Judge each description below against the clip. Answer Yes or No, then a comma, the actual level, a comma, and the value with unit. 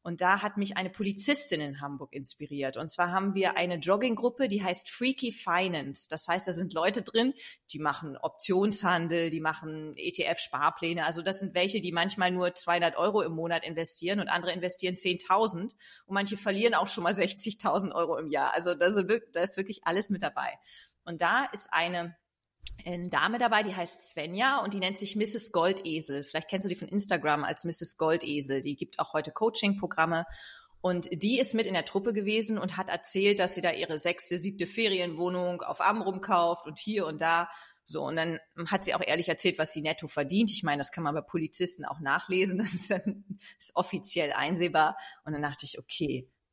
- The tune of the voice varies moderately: Yes, average, 3.3 semitones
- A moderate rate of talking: No, fast, 195 wpm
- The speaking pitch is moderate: Yes, medium, 180 Hz